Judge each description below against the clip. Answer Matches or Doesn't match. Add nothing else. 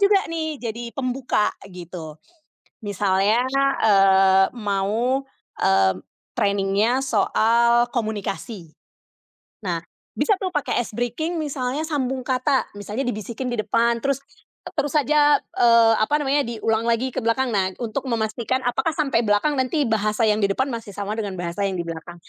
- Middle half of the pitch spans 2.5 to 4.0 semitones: Doesn't match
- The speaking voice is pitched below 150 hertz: Doesn't match